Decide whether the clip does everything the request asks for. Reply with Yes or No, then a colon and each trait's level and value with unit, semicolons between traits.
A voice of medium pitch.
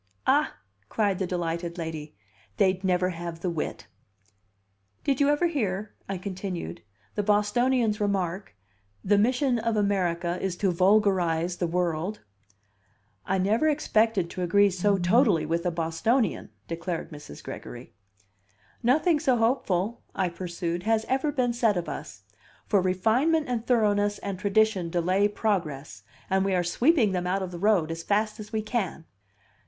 No: high, 195 Hz